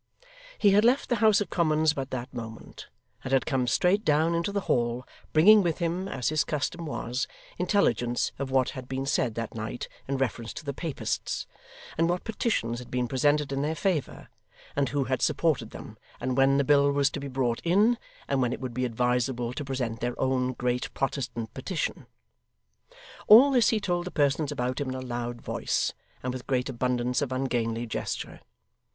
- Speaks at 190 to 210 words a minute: Yes, average, 195 wpm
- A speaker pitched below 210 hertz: Yes, low, 135 Hz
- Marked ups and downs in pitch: No, average, 4.5 semitones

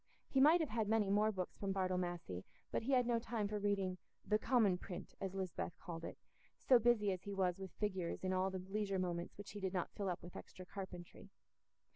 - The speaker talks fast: Yes, fast, 225 wpm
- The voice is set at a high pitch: Yes, high, 195 Hz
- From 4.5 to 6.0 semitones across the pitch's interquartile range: No, narrow, 2.6 semitones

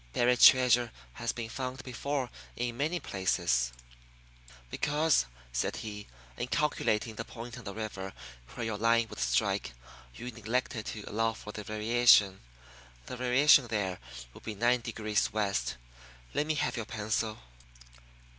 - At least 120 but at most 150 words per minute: Yes, average, 145 wpm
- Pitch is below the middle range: Yes, low, 115 Hz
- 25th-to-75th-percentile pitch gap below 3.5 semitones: Yes, average, 2.9 semitones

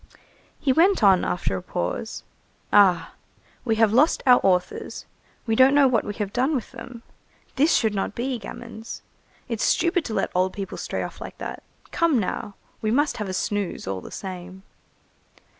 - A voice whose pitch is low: No, high, 220 Hz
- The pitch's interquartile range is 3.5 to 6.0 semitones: Yes, average, 5.2 semitones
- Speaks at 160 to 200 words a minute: Yes, average, 175 wpm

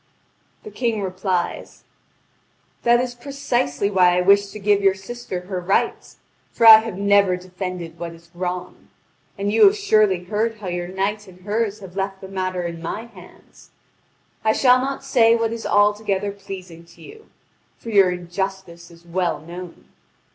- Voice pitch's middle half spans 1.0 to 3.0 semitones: No, average, 3.4 semitones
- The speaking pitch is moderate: No, high, 195 Hz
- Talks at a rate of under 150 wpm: No, average, 165 wpm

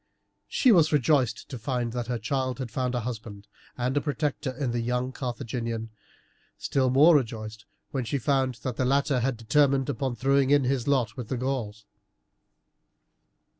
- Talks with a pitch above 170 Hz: No, low, 130 Hz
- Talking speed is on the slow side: No, average, 165 wpm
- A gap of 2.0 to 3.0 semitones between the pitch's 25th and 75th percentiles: Yes, average, 2.7 semitones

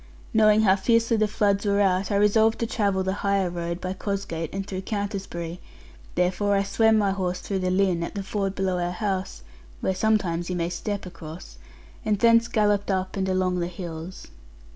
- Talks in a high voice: Yes, high, 195 Hz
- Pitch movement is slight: Yes, narrow, 2.3 semitones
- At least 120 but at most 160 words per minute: No, average, 190 wpm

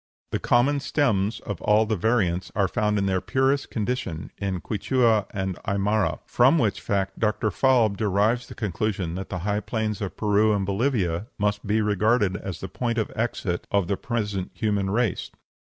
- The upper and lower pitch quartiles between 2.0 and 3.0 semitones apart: Yes, average, 2.7 semitones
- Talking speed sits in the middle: Yes, average, 175 wpm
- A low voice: Yes, low, 105 Hz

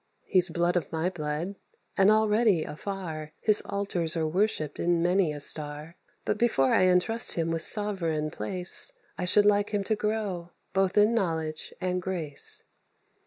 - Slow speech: No, average, 160 wpm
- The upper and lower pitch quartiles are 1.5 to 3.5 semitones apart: No, average, 4.1 semitones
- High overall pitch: No, medium, 180 Hz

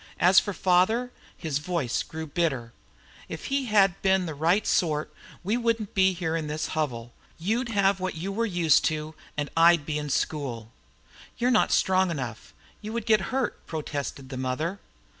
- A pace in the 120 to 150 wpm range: No, average, 175 wpm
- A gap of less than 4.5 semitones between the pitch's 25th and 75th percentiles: No, average, 4.8 semitones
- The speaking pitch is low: No, medium, 170 Hz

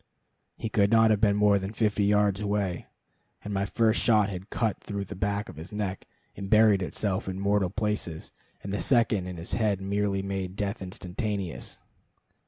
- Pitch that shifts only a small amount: Yes, narrow, 1.6 semitones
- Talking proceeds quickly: No, average, 185 wpm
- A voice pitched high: No, low, 100 Hz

